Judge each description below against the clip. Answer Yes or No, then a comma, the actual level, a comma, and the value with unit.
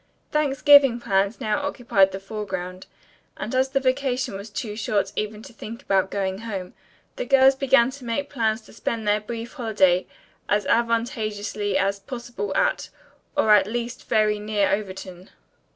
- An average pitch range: Yes, average, 3.5 semitones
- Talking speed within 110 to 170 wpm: Yes, average, 155 wpm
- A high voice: Yes, high, 215 Hz